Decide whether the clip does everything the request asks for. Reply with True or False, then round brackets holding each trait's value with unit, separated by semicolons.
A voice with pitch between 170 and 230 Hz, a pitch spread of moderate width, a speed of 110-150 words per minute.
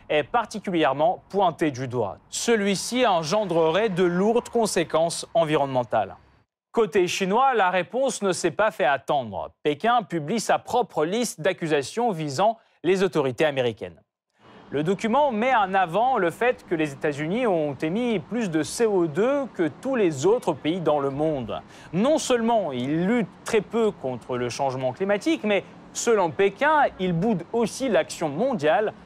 False (190 Hz; 6.7 semitones; 145 wpm)